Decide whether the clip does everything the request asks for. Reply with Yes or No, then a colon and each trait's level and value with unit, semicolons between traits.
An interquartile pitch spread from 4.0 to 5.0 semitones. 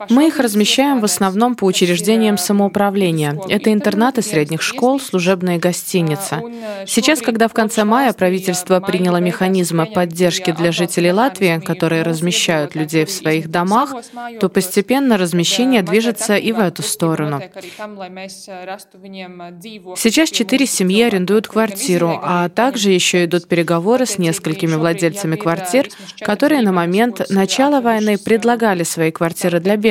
Yes: average, 4.3 semitones